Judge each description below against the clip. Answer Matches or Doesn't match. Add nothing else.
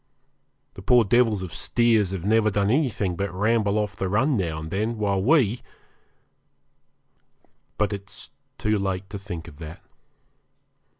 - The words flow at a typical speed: Matches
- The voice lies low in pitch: Matches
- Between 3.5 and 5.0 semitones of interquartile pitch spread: Doesn't match